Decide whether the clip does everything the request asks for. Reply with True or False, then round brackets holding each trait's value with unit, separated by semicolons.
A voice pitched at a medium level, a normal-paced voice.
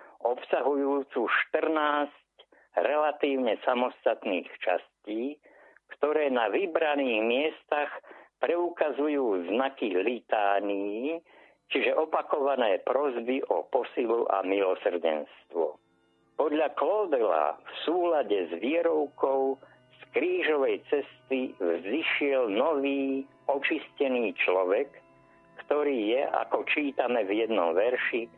False (150 Hz; 80 wpm)